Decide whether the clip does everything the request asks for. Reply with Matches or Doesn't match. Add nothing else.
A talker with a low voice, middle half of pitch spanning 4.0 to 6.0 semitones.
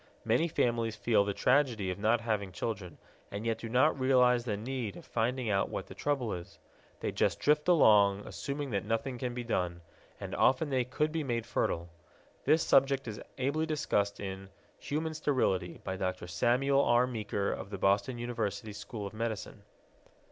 Matches